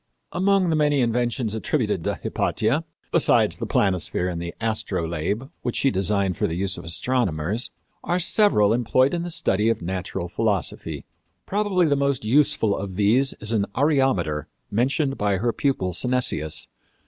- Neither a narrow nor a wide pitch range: No, wide, 6.3 semitones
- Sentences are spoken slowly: No, average, 150 wpm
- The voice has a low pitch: Yes, low, 115 Hz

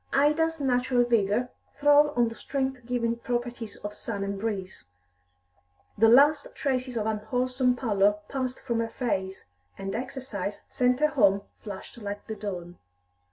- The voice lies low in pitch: No, high, 240 Hz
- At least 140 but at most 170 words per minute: Yes, average, 145 wpm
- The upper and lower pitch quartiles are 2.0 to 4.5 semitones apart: Yes, average, 3.9 semitones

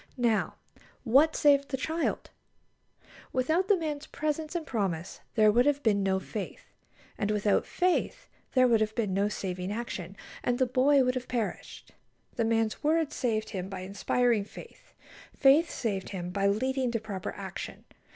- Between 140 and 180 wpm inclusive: Yes, average, 160 wpm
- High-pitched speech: Yes, high, 230 Hz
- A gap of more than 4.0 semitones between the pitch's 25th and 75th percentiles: Yes, wide, 5.6 semitones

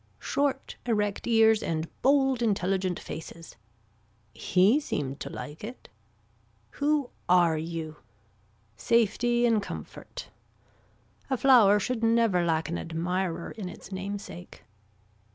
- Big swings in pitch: Yes, wide, 5.8 semitones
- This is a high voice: Yes, high, 200 Hz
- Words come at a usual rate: No, slow, 110 wpm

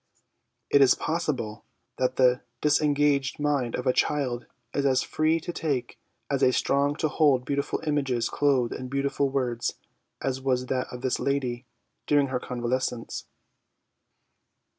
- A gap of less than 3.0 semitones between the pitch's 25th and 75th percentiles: Yes, narrow, 2.5 semitones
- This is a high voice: No, low, 135 Hz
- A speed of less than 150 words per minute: Yes, average, 140 wpm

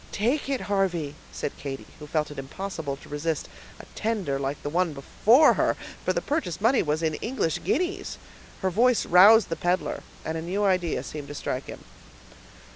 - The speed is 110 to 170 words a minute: No, average, 185 wpm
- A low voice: No, medium, 175 Hz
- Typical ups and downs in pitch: No, wide, 6.7 semitones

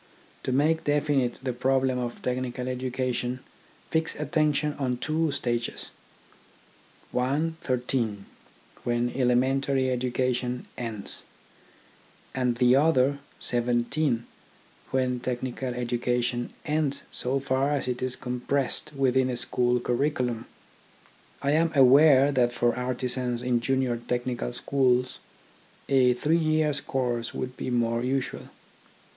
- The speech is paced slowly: Yes, slow, 115 wpm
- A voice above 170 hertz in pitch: No, low, 125 Hz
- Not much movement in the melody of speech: Yes, narrow, 2.1 semitones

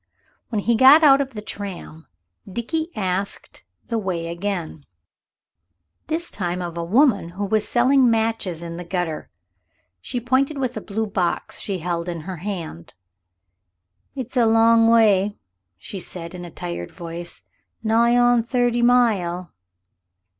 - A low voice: No, high, 205 Hz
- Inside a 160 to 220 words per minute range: No, average, 145 wpm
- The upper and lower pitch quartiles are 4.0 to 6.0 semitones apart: Yes, wide, 5.4 semitones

